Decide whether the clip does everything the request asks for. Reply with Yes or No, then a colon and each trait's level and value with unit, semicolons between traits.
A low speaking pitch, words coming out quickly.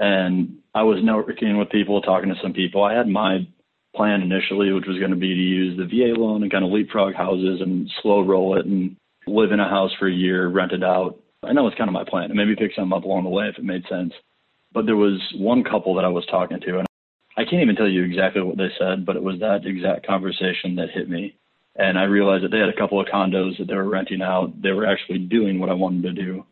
Yes: very low, 95 Hz; fast, 265 wpm